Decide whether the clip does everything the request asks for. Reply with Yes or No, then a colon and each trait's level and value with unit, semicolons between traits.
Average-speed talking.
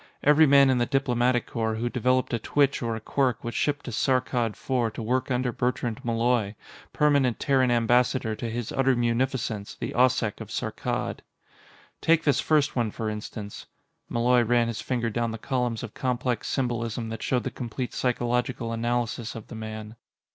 Yes: average, 175 wpm